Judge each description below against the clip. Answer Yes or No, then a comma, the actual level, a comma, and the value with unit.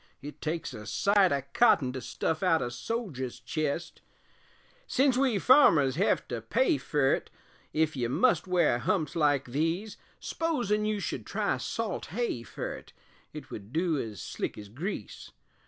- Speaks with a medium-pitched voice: Yes, medium, 160 Hz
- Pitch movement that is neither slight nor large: No, wide, 8.1 semitones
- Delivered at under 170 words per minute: Yes, average, 155 wpm